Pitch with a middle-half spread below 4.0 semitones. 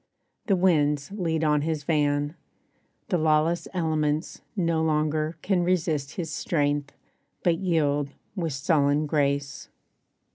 Yes: narrow, 2.4 semitones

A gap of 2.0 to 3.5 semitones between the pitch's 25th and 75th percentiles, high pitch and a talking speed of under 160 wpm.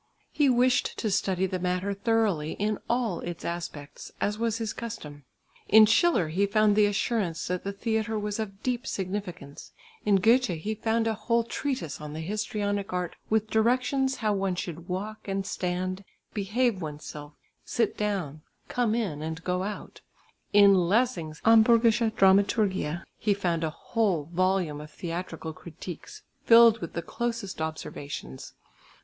No: average, 4.4 semitones; high, 200 Hz; average, 150 wpm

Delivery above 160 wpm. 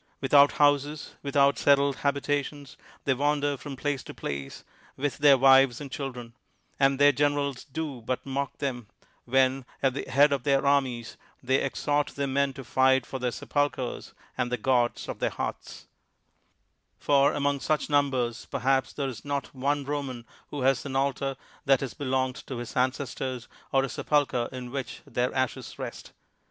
Yes: average, 170 wpm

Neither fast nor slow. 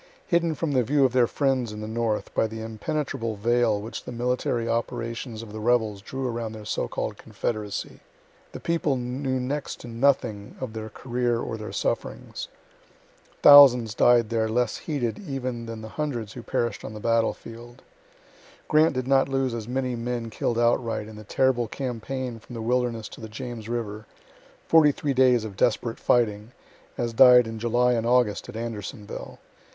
Yes: average, 175 wpm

